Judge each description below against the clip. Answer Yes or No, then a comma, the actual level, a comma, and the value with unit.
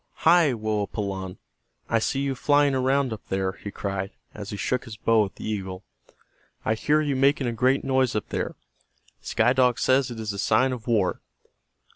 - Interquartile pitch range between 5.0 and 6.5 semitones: No, average, 4.4 semitones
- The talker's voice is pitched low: Yes, low, 115 Hz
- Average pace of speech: Yes, average, 185 wpm